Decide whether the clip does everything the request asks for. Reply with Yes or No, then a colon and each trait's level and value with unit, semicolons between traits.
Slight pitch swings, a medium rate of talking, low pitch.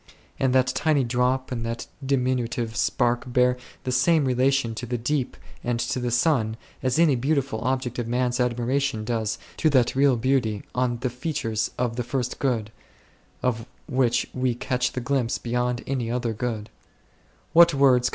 Yes: narrow, 1.8 semitones; average, 160 wpm; low, 125 Hz